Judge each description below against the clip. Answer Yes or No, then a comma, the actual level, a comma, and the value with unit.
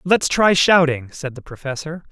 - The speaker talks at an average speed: Yes, average, 170 wpm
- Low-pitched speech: No, medium, 155 Hz